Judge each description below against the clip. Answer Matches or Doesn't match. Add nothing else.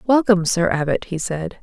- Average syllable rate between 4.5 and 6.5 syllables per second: Matches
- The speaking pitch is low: Doesn't match